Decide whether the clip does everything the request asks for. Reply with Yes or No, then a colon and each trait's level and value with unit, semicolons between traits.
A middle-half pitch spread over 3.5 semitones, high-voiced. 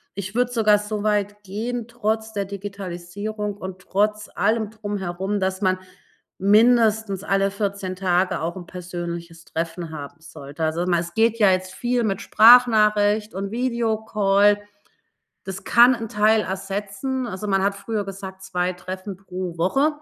No: narrow, 2.6 semitones; high, 200 Hz